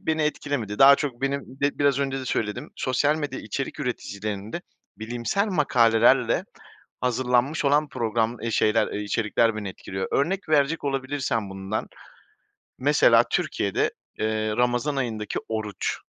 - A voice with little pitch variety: No, average, 4.5 semitones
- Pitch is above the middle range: No, low, 125 Hz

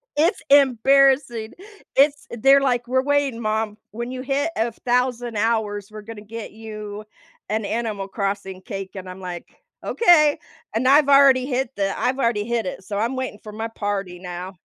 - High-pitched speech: Yes, high, 230 Hz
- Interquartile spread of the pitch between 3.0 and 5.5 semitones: Yes, average, 4.2 semitones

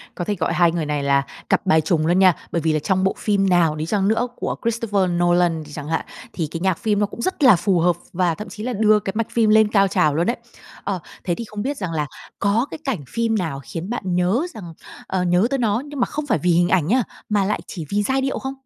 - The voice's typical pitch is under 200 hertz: Yes, high, 190 Hz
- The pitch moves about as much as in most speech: Yes, average, 4.4 semitones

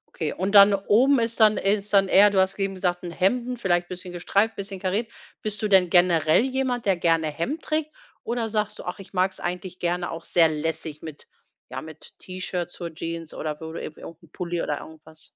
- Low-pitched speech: No, medium, 185 Hz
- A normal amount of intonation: Yes, average, 3.7 semitones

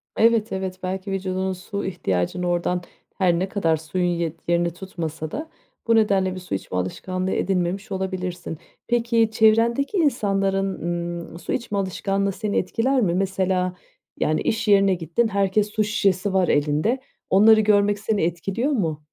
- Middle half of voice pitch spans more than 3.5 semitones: No, average, 3.1 semitones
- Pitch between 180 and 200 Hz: Yes, high, 190 Hz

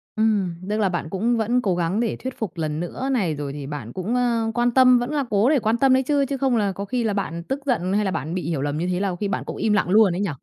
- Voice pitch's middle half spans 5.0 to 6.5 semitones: Yes, wide, 5.5 semitones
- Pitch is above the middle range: Yes, high, 210 Hz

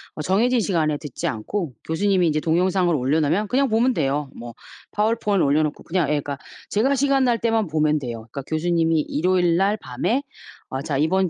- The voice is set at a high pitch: No, medium, 170 Hz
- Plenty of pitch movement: Yes, wide, 5.7 semitones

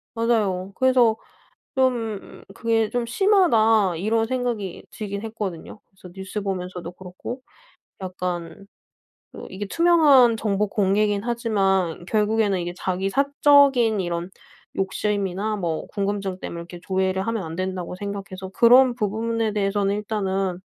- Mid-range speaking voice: No, high, 205 Hz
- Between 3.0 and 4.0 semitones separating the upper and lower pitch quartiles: Yes, average, 3.3 semitones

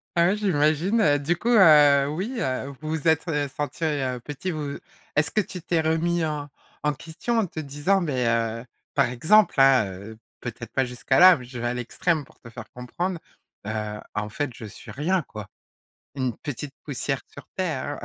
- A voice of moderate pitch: Yes, medium, 145 Hz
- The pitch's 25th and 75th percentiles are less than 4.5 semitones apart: No, average, 5.1 semitones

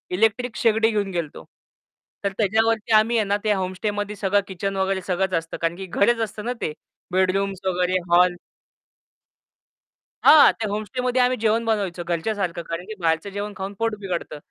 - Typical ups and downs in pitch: Yes, average, 3.1 semitones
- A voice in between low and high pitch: No, high, 200 Hz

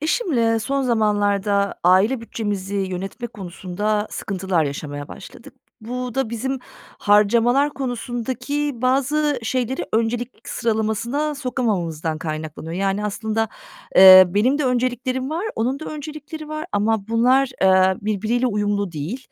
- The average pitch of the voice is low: No, high, 225 Hz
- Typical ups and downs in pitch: Yes, average, 4.6 semitones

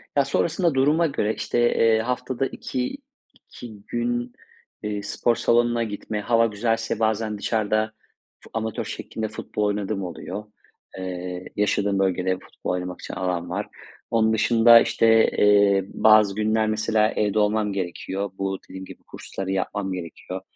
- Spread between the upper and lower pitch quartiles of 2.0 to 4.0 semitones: Yes, average, 2.8 semitones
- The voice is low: Yes, low, 110 Hz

